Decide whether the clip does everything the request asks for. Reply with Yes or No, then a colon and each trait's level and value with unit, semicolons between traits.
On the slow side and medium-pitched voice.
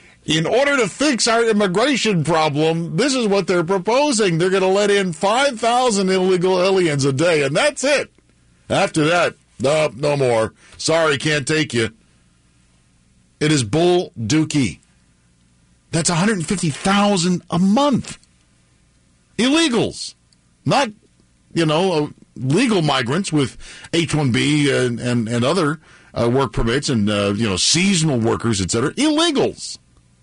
Yes: slow, 130 wpm; medium, 155 Hz